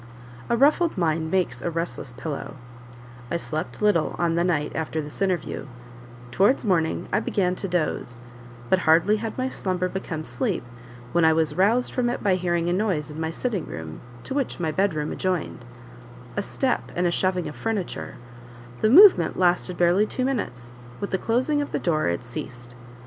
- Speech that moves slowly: No, average, 180 wpm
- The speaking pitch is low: No, medium, 175 Hz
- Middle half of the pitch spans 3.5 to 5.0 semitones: Yes, average, 4.6 semitones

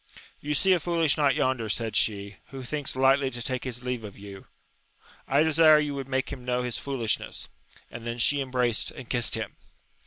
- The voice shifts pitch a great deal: No, average, 3.1 semitones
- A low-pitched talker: Yes, low, 130 Hz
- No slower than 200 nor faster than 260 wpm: Yes, fast, 205 wpm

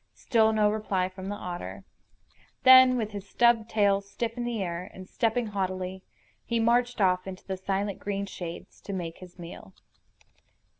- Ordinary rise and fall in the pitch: Yes, average, 3.3 semitones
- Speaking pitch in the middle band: No, high, 200 Hz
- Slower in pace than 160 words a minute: No, average, 165 wpm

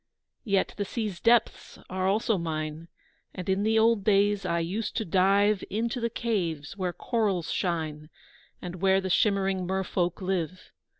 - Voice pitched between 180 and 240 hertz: Yes, high, 190 Hz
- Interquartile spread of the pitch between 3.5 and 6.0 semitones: No, average, 3.0 semitones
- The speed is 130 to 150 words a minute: No, average, 160 wpm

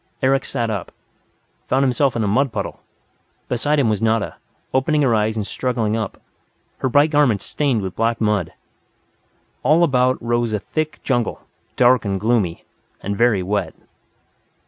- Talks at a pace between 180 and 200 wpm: No, average, 155 wpm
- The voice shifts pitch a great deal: No, average, 3.8 semitones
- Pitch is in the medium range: No, low, 120 Hz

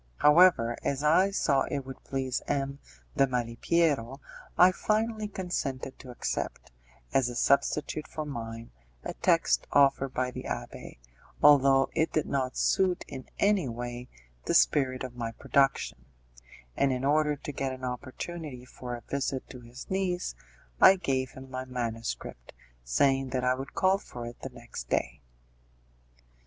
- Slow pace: No, average, 150 wpm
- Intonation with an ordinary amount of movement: Yes, average, 3.3 semitones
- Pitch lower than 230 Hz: Yes, low, 135 Hz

